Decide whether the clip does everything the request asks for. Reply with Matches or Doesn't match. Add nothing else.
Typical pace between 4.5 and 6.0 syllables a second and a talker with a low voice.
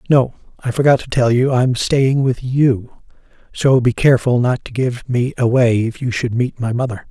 Matches